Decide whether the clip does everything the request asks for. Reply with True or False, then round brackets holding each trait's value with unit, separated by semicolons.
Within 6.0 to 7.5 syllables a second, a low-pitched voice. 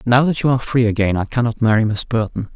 True (6.6 syllables/s; 115 Hz)